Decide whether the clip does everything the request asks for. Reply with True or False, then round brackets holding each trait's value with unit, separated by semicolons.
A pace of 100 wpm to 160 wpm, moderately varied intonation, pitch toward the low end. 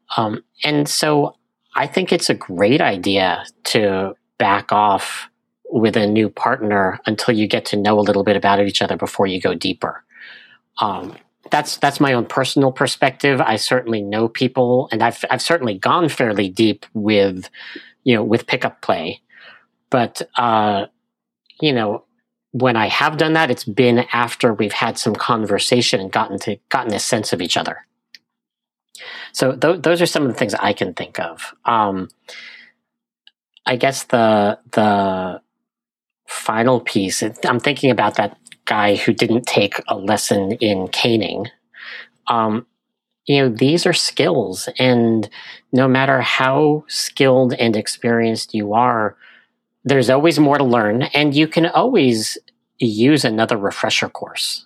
True (155 wpm; 4.1 semitones; 120 Hz)